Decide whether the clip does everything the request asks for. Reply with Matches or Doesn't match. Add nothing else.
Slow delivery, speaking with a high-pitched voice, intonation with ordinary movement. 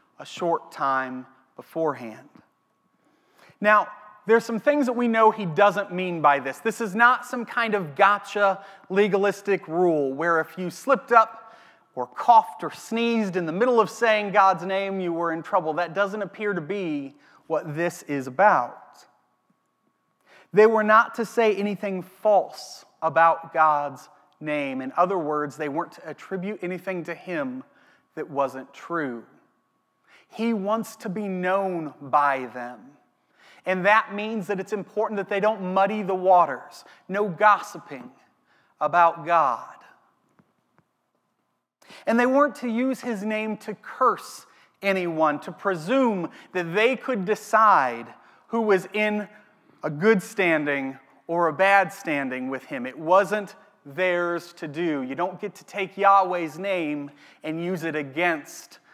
Doesn't match